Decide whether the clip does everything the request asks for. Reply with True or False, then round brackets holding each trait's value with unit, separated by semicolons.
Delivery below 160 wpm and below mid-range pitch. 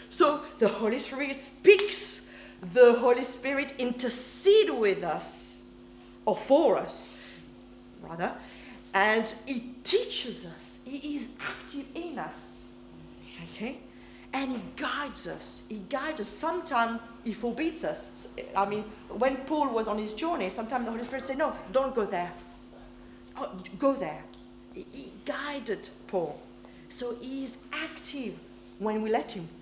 False (140 wpm; 235 Hz)